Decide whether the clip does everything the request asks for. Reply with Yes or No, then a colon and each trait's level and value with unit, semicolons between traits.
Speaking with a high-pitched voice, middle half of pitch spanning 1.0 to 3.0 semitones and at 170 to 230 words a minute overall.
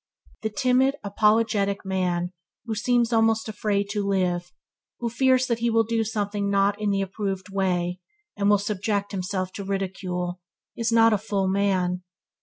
No: high, 200 Hz; average, 2.7 semitones; average, 160 wpm